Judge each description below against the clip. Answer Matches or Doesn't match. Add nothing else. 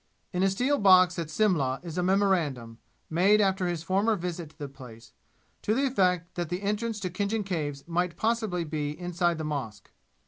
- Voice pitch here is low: Doesn't match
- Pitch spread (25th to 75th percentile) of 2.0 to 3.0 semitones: Doesn't match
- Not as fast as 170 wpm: Doesn't match